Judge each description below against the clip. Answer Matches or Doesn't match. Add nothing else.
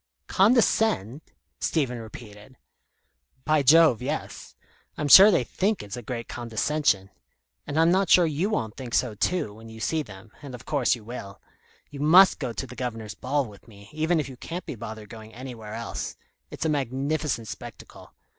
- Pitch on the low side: Matches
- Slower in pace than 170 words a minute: Doesn't match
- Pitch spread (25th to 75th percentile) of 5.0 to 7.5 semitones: Matches